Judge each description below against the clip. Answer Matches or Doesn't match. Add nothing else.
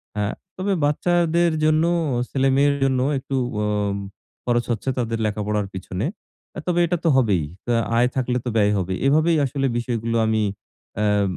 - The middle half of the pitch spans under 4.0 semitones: Doesn't match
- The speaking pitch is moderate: Doesn't match